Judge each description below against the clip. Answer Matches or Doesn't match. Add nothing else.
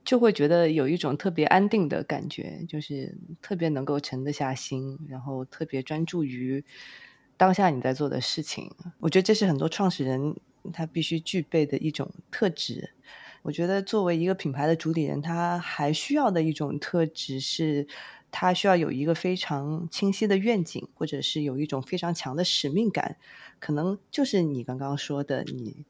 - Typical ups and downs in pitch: Matches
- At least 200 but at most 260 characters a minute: Doesn't match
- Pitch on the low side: Doesn't match